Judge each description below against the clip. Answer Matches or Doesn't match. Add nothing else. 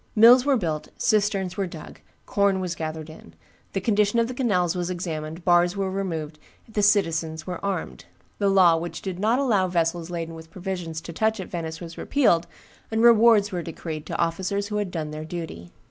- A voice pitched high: Doesn't match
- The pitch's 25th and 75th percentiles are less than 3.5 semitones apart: Doesn't match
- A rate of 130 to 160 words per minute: Doesn't match